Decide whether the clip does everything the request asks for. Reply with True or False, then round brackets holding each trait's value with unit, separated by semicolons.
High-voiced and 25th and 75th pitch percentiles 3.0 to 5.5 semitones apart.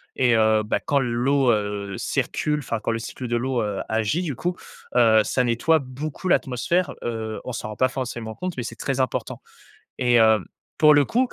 False (120 Hz; 3.9 semitones)